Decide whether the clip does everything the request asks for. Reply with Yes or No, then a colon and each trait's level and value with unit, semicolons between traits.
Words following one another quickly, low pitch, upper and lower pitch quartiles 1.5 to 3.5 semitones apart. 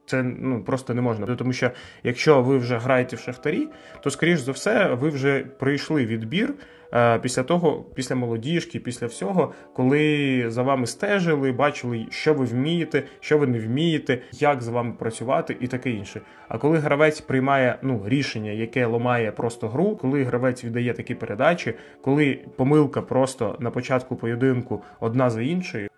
Yes: fast, 160 wpm; low, 130 Hz; average, 3.1 semitones